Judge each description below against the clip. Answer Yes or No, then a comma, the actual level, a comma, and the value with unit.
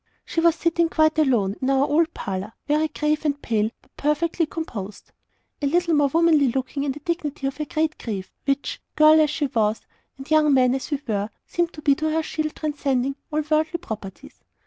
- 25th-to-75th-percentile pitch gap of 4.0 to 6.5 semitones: No, average, 3.0 semitones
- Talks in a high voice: Yes, very high, 295 Hz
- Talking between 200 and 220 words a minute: Yes, fast, 205 wpm